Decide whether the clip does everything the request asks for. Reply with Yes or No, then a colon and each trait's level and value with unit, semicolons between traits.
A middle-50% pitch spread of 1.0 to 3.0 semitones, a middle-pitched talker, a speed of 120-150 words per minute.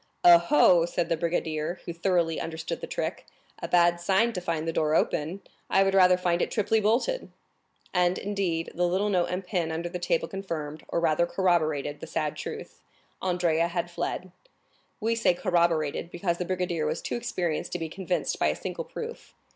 No: narrow, 2.4 semitones; medium, 175 Hz; average, 185 wpm